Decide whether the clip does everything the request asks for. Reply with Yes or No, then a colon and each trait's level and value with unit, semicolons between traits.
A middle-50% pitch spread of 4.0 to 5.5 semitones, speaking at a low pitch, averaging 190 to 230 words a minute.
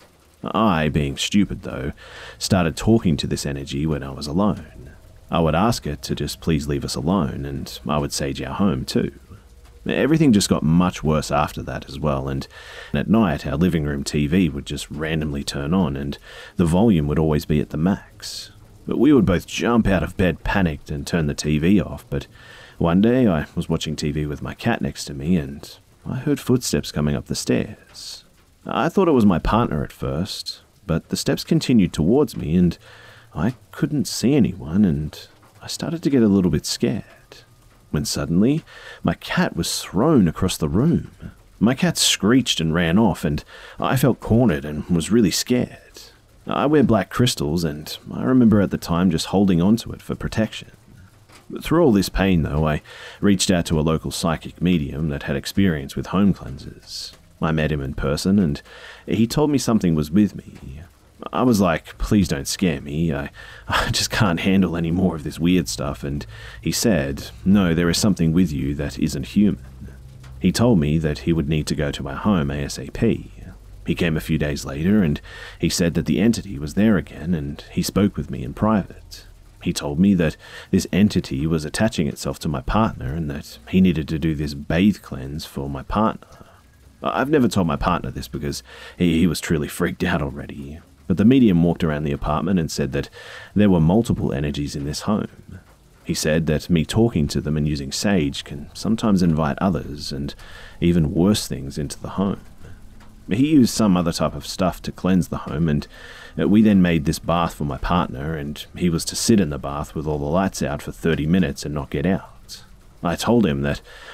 Yes: average, 4.8 semitones; very low, 80 Hz; average, 200 wpm